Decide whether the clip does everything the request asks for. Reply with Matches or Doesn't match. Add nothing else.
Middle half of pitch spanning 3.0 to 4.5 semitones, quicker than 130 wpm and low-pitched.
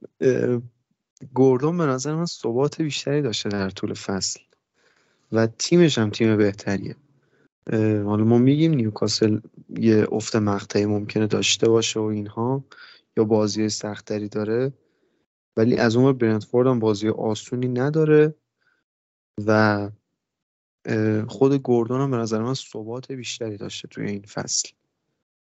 Doesn't match